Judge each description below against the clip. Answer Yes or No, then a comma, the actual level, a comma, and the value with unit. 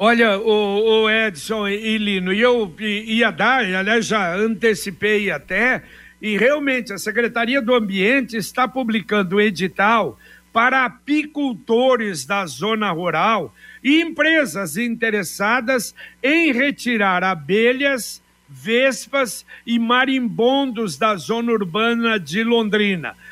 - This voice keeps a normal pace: No, slow, 105 wpm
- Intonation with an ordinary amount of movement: Yes, average, 3.5 semitones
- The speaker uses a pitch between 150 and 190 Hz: No, high, 225 Hz